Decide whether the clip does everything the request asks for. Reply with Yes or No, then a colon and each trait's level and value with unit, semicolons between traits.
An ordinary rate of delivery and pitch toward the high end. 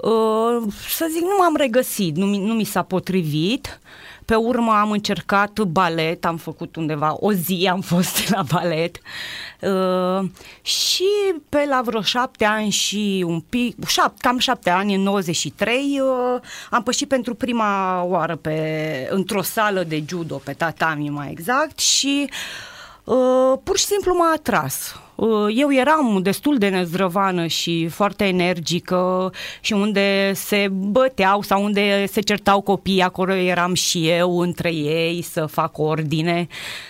Yes: average, 145 wpm; high, 195 Hz